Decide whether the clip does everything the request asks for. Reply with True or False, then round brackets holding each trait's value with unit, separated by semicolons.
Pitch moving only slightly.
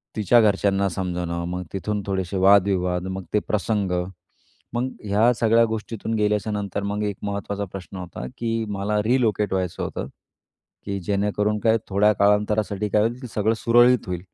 True (1.9 semitones)